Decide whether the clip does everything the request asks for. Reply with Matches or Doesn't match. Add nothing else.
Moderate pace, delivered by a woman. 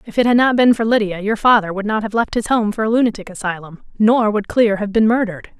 Doesn't match